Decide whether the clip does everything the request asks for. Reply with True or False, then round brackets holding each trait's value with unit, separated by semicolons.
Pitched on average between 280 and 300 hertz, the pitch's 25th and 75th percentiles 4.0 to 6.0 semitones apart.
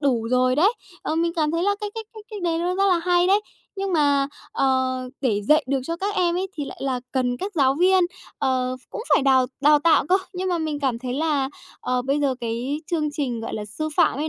True (295 Hz; 5.2 semitones)